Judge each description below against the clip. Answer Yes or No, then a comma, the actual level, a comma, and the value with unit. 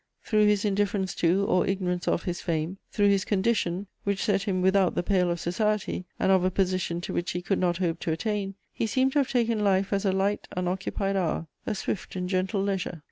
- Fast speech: Yes, fast, 220 wpm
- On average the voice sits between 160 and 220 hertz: Yes, high, 190 Hz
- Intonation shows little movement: Yes, narrow, 2.2 semitones